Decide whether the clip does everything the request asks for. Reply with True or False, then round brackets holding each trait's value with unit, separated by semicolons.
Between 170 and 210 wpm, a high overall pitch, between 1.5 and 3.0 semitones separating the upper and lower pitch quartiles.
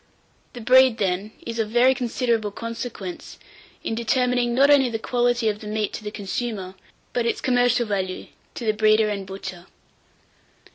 False (160 wpm; 225 Hz; 2.7 semitones)